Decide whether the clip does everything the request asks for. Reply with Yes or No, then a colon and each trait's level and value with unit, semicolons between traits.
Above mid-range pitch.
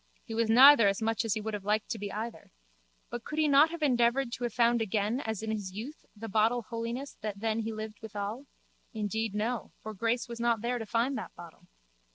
Yes: high, 225 Hz